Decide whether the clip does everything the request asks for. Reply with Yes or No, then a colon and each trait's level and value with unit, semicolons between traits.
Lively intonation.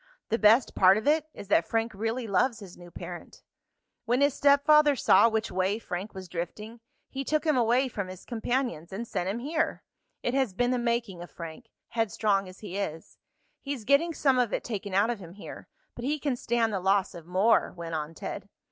No: average, 5.0 semitones